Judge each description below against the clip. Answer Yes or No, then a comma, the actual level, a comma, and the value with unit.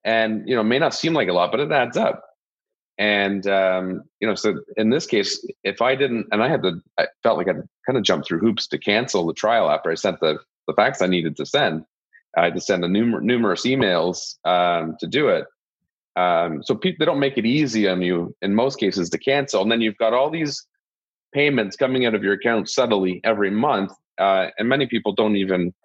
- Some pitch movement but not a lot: No, wide, 6.7 semitones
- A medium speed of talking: No, fast, 230 wpm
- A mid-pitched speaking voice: No, low, 110 Hz